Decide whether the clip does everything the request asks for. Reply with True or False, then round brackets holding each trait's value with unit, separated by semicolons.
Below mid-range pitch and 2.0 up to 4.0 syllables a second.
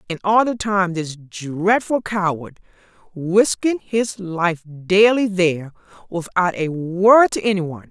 False (185 Hz; 3.9 syllables/s)